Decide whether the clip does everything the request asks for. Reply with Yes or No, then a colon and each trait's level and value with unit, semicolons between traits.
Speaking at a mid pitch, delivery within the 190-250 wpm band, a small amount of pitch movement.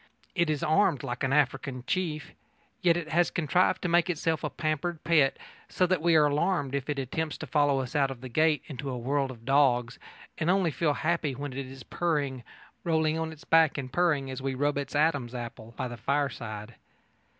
No: medium, 145 Hz; fast, 205 wpm; average, 3.6 semitones